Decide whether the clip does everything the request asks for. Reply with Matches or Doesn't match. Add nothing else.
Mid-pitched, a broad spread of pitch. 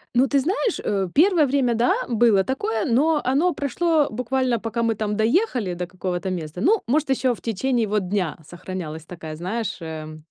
Doesn't match